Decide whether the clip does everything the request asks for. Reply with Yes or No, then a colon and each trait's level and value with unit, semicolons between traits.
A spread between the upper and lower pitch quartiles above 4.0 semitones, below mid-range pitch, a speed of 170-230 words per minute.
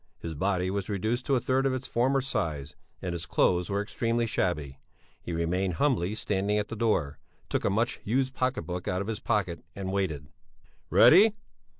Yes: average, 5.2 semitones; low, 100 Hz; average, 190 wpm